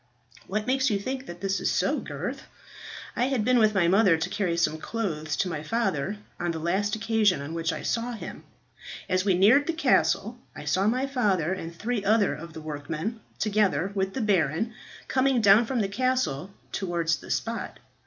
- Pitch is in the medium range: No, high, 200 Hz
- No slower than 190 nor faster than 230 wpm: Yes, average, 195 wpm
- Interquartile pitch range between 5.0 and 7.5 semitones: Yes, average, 5.3 semitones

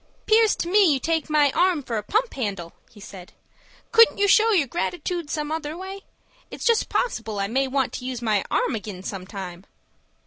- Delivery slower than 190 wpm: No, average, 200 wpm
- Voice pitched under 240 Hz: No, very high, 290 Hz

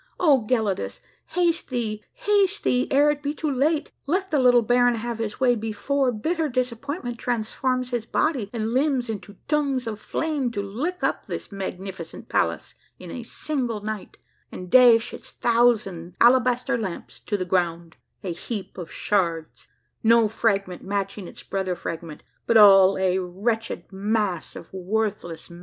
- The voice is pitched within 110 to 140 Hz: No, high, 225 Hz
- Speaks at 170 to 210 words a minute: No, average, 160 wpm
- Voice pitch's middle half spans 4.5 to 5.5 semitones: Yes, average, 4.8 semitones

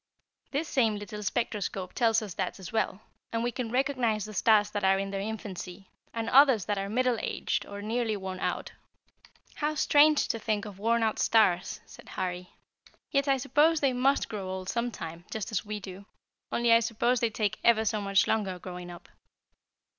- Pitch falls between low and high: No, high, 215 Hz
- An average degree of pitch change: Yes, average, 3.4 semitones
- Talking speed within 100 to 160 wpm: No, average, 190 wpm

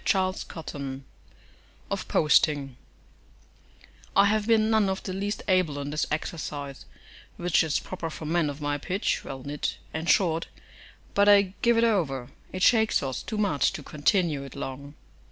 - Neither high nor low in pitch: Yes, medium, 165 Hz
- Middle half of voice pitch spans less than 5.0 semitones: No, wide, 5.6 semitones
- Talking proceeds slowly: No, average, 160 wpm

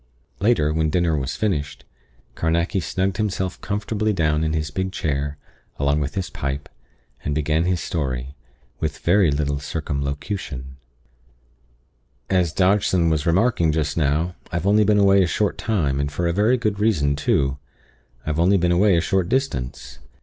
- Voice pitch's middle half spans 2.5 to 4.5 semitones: No, average, 5.1 semitones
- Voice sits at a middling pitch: No, very low, 85 Hz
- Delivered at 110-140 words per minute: No, average, 155 wpm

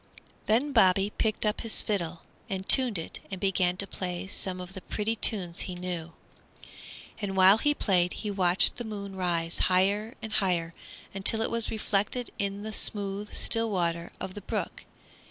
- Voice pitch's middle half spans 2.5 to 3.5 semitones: Yes, average, 2.8 semitones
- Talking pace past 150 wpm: Yes, average, 170 wpm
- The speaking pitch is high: Yes, high, 195 Hz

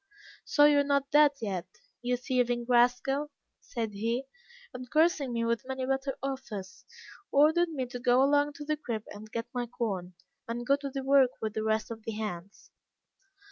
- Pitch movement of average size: Yes, average, 3.8 semitones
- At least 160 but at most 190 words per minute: Yes, average, 180 wpm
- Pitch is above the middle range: Yes, very high, 250 Hz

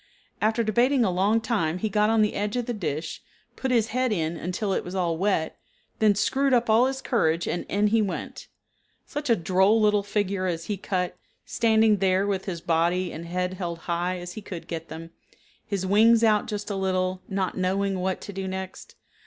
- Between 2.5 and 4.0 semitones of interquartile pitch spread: Yes, average, 3.2 semitones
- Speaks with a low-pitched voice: No, high, 195 Hz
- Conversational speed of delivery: No, fast, 210 wpm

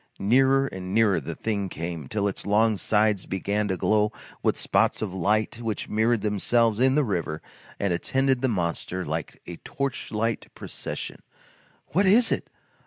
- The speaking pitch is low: Yes, low, 105 Hz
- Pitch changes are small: No, average, 3.9 semitones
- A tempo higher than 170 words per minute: No, average, 160 wpm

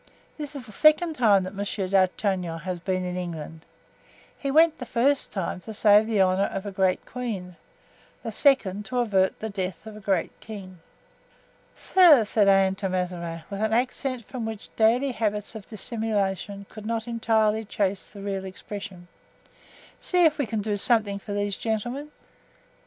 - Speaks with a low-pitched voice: No, high, 205 Hz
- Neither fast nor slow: Yes, average, 170 wpm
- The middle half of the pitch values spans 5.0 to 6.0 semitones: No, average, 3.3 semitones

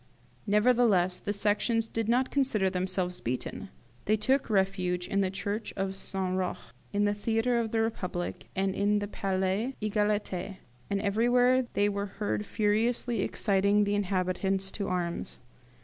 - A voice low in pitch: No, high, 205 Hz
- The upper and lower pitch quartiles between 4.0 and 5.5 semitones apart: No, narrow, 2.6 semitones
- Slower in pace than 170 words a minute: Yes, average, 150 wpm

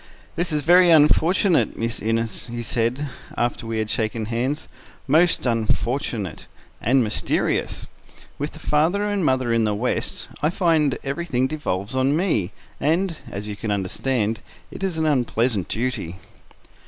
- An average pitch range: No, wide, 5.7 semitones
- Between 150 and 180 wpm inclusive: No, average, 140 wpm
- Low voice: Yes, low, 130 Hz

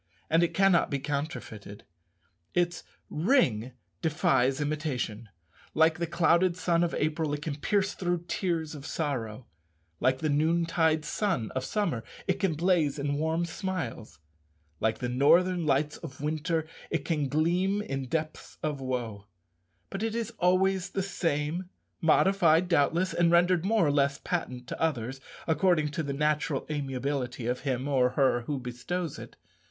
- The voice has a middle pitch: Yes, medium, 155 Hz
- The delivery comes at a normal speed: Yes, average, 150 wpm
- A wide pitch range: No, average, 4.2 semitones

